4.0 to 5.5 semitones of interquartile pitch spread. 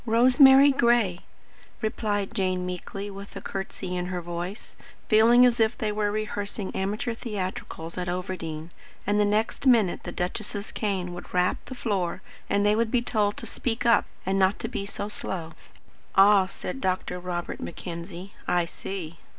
No: average, 3.3 semitones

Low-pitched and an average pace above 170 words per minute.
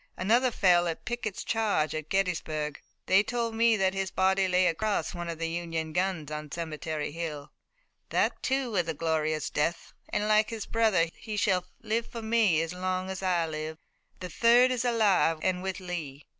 No: medium, 185 Hz; average, 185 wpm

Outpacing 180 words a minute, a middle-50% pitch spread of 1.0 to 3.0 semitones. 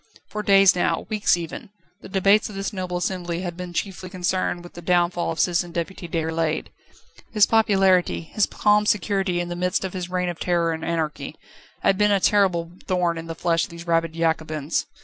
Yes: average, 195 wpm; narrow, 2.4 semitones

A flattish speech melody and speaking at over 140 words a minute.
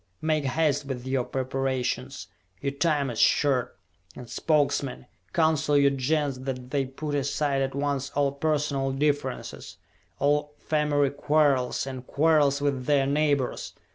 No: narrow, 1.8 semitones; slow, 135 wpm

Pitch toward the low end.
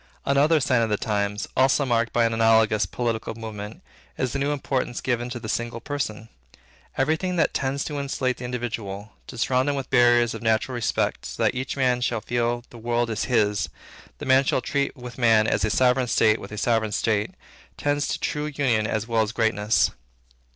Yes: low, 120 Hz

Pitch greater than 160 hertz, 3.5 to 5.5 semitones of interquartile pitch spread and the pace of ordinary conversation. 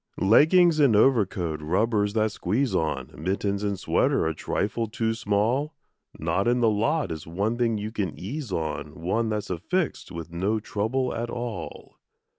No: low, 105 Hz; average, 4.5 semitones; average, 160 wpm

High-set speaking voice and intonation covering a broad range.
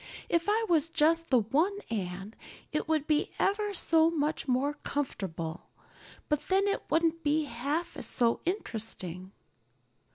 Yes: very high, 300 Hz; wide, 6.2 semitones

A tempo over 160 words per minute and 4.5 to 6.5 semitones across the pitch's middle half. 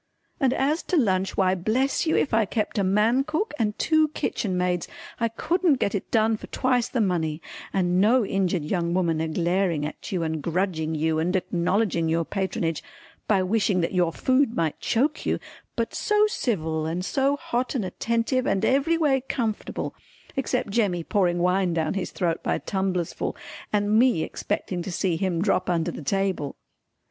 Yes: average, 180 wpm; wide, 5.5 semitones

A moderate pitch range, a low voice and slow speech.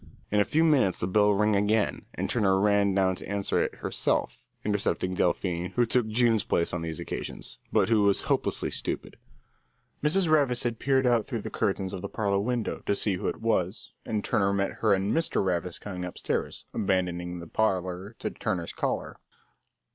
No: average, 3.3 semitones; low, 100 Hz; average, 185 wpm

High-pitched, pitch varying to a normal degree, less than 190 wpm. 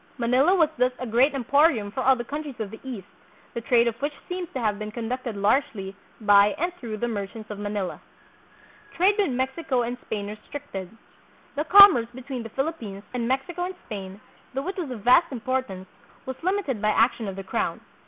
No: high, 245 Hz; average, 4.8 semitones; average, 200 wpm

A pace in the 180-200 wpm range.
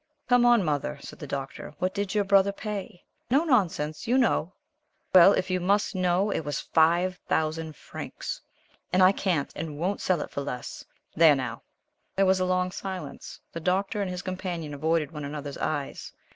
Yes: average, 185 wpm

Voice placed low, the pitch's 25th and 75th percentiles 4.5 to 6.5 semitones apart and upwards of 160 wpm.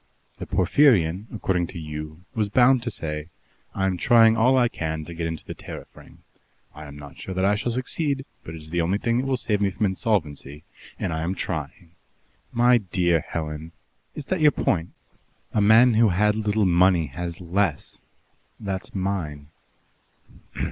Yes: very low, 95 Hz; wide, 5.5 semitones; average, 180 wpm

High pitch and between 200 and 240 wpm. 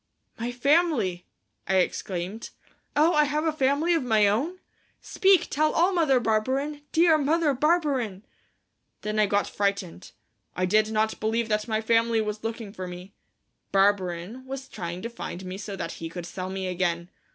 No: high, 220 Hz; average, 165 wpm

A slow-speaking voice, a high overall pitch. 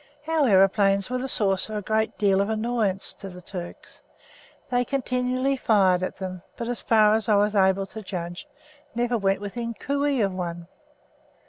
No: average, 180 wpm; high, 210 Hz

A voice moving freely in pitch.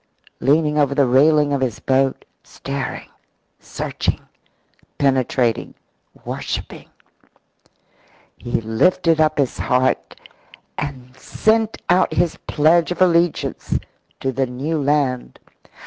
No: average, 3.4 semitones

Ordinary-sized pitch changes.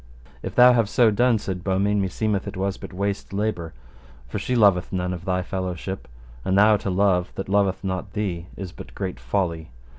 No: narrow, 2.1 semitones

